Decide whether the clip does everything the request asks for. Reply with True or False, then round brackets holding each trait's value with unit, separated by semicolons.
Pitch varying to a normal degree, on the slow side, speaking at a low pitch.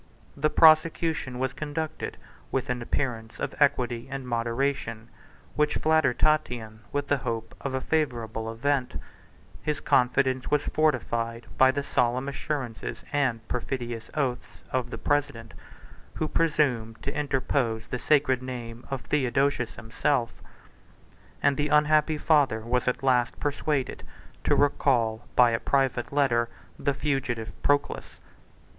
True (3.6 semitones; 130 wpm; 130 Hz)